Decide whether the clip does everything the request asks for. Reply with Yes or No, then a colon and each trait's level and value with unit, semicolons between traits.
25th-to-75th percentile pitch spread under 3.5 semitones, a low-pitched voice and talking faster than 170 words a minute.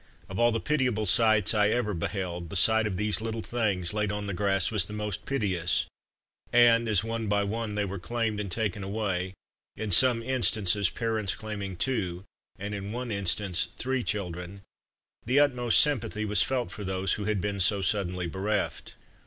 Yes: average, 2.8 semitones; low, 105 Hz; average, 180 wpm